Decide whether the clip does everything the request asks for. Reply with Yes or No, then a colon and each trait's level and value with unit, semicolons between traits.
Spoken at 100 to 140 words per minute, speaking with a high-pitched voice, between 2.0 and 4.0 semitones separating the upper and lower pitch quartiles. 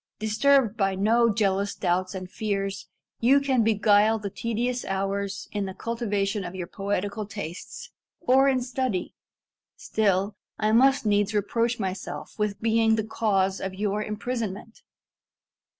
Yes: slow, 135 wpm; high, 210 Hz; average, 2.7 semitones